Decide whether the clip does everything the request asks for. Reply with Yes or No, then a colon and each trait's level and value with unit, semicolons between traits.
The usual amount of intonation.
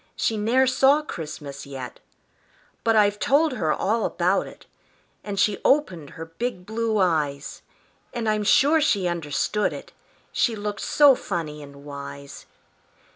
No: wide, 7.1 semitones